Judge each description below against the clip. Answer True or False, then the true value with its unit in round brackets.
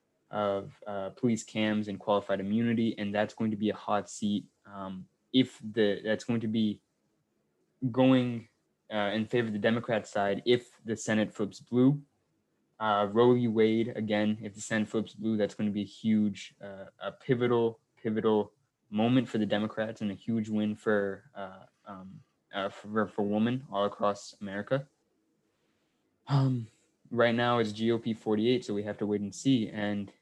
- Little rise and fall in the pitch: True (2.3 semitones)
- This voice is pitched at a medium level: False (110 Hz)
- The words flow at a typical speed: True (175 wpm)